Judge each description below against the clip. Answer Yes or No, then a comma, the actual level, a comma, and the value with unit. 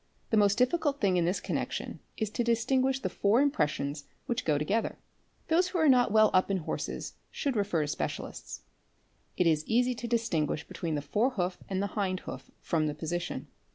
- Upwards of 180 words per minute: Yes, average, 190 wpm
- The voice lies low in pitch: No, high, 205 Hz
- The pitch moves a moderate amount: No, wide, 6.4 semitones